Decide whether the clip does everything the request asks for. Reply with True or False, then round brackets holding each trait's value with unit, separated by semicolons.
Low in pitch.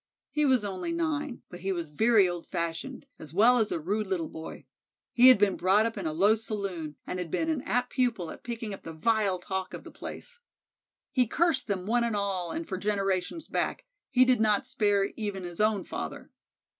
False (205 Hz)